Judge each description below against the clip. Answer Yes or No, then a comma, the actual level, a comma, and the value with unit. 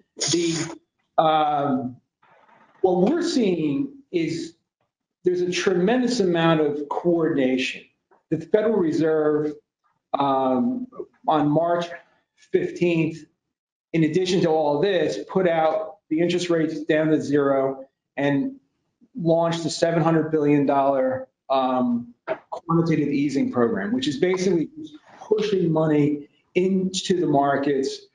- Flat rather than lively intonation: No, average, 4.4 semitones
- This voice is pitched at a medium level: Yes, medium, 165 Hz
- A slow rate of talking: Yes, slow, 105 wpm